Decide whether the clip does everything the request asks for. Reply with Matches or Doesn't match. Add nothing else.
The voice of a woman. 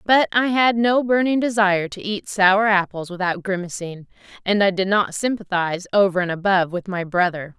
Matches